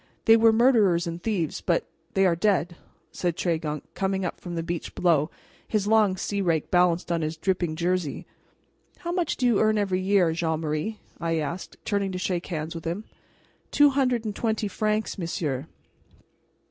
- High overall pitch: No, medium, 180 Hz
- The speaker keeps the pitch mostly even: No, average, 4.3 semitones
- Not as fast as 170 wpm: No, average, 175 wpm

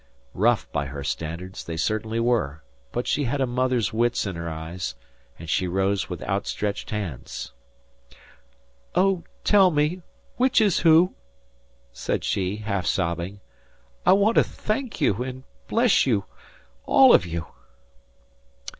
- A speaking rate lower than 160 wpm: Yes, average, 140 wpm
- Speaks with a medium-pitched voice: No, low, 105 Hz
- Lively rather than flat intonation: Yes, wide, 8.8 semitones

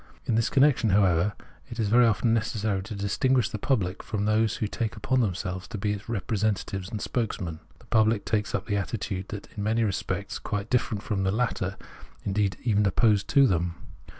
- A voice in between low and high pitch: No, low, 105 Hz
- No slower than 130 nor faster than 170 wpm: No, average, 185 wpm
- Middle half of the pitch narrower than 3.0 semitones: Yes, narrow, 2.6 semitones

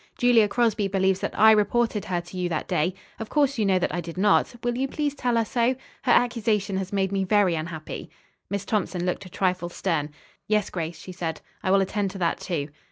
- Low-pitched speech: No, high, 195 Hz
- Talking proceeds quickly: Yes, fast, 225 wpm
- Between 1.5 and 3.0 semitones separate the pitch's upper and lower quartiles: No, average, 3.7 semitones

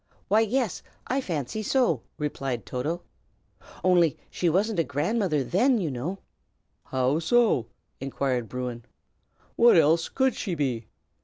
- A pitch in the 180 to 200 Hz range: No, medium, 165 Hz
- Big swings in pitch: Yes, wide, 8.0 semitones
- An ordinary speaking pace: No, slow, 130 wpm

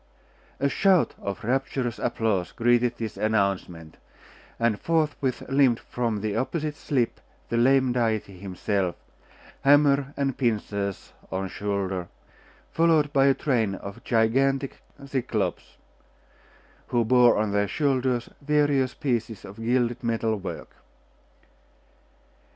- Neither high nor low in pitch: No, low, 120 Hz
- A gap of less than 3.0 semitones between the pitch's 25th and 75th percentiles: No, average, 4.8 semitones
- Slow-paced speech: Yes, slow, 110 wpm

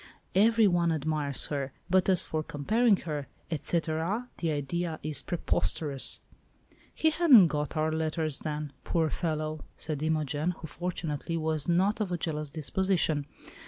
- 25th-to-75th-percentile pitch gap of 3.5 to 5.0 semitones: No, average, 2.9 semitones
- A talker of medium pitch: Yes, medium, 160 Hz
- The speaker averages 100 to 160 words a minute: Yes, average, 145 wpm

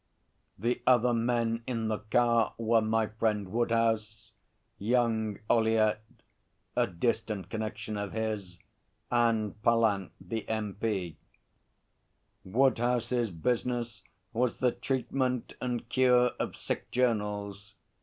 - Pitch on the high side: No, low, 115 Hz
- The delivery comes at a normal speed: No, slow, 105 wpm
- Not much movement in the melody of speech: Yes, narrow, 2.0 semitones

